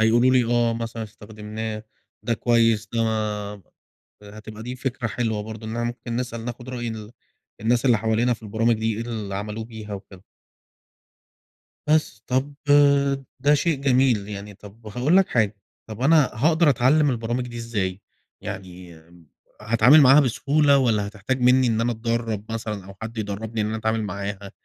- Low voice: Yes, low, 115 Hz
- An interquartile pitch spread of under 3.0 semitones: Yes, narrow, 2.5 semitones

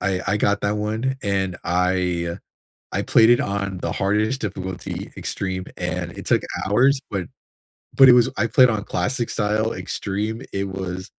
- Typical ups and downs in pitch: Yes, average, 3.0 semitones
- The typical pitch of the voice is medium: No, low, 100 Hz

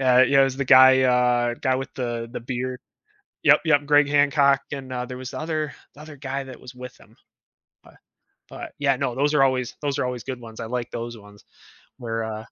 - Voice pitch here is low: Yes, low, 130 Hz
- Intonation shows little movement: Yes, narrow, 2.2 semitones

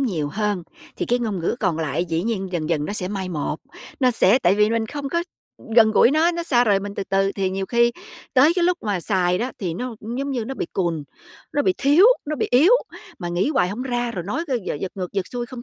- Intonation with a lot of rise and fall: Yes, wide, 5.8 semitones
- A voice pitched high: Yes, high, 210 Hz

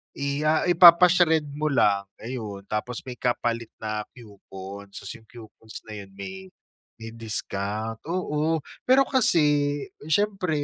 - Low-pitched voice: Yes, low, 120 Hz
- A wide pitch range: Yes, wide, 6.8 semitones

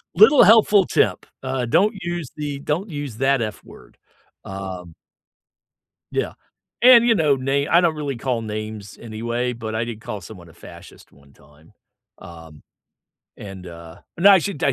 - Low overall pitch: Yes, low, 120 Hz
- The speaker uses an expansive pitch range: Yes, wide, 8.0 semitones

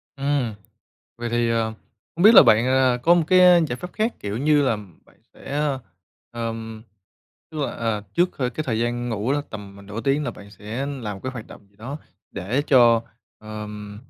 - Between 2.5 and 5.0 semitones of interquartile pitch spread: Yes, average, 4.4 semitones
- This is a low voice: Yes, low, 120 Hz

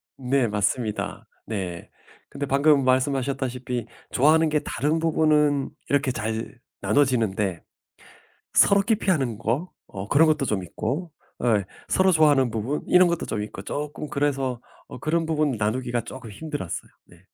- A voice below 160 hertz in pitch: Yes, low, 135 Hz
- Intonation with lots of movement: No, average, 4.9 semitones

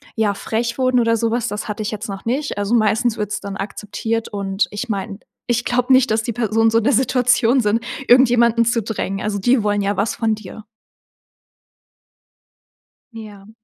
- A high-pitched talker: Yes, high, 225 Hz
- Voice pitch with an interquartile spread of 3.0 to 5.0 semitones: No, narrow, 2.5 semitones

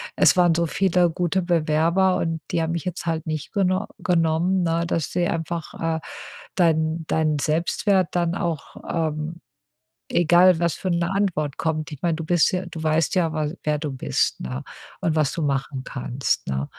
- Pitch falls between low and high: Yes, medium, 165 Hz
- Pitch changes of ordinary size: No, narrow, 2.1 semitones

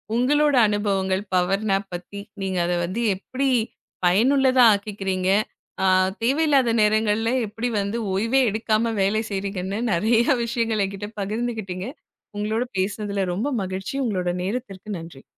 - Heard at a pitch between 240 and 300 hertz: No, high, 210 Hz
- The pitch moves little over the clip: No, average, 3.3 semitones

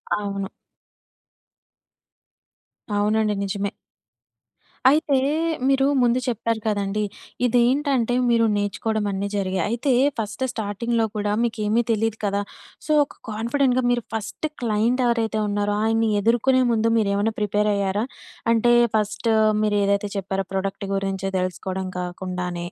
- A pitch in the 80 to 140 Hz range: No, high, 215 Hz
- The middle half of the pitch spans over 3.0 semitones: No, average, 2.7 semitones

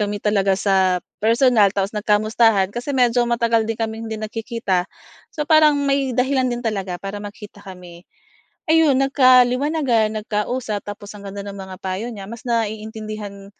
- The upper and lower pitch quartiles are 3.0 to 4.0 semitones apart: Yes, average, 3.3 semitones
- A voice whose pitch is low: No, high, 220 Hz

